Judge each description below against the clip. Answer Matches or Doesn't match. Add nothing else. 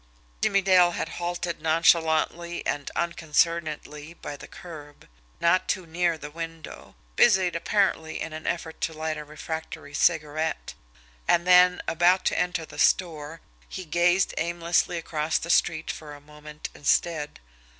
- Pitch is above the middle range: Doesn't match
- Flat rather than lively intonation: Matches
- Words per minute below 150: Matches